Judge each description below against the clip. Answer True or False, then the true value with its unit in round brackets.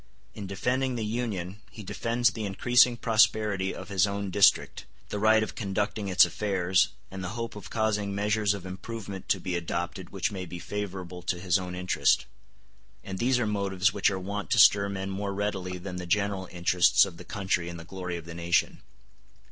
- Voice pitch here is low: True (100 Hz)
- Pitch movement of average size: False (2.3 semitones)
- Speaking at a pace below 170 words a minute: False (195 wpm)